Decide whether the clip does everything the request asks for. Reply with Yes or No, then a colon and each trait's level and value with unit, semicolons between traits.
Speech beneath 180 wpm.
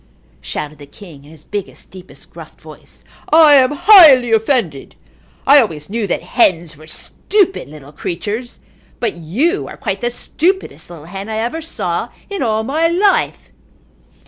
Yes: average, 155 wpm